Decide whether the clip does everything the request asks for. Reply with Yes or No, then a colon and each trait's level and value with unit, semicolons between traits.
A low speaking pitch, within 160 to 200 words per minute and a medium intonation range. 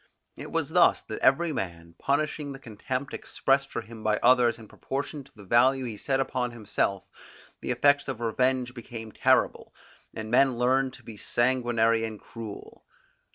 Yes: low, 125 Hz; average, 165 wpm; average, 3.1 semitones